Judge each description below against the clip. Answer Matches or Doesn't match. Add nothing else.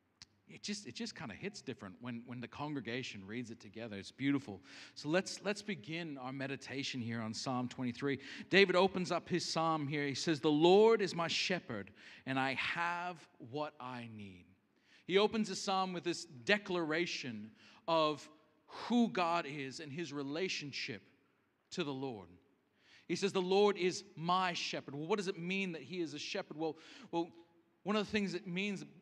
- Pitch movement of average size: Doesn't match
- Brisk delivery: Doesn't match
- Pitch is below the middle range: Doesn't match